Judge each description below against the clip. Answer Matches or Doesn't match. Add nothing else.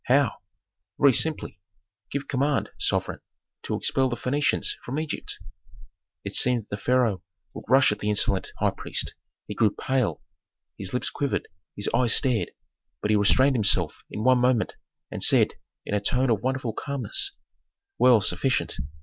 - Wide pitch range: Doesn't match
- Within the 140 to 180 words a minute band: Matches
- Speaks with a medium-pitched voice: Doesn't match